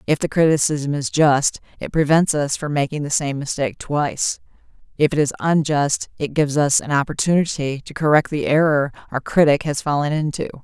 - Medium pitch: Yes, medium, 145 Hz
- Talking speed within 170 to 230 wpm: Yes, average, 180 wpm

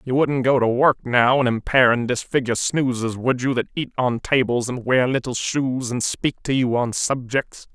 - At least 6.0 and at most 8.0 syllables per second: No, 4.8 syllables/s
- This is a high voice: No, low, 125 Hz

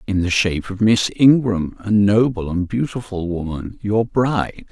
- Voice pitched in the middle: No, low, 100 Hz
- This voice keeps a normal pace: Yes, average, 155 wpm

